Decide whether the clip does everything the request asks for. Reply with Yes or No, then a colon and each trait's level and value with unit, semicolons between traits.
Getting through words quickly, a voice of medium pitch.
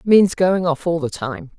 Yes: fast, 225 wpm; medium, 165 Hz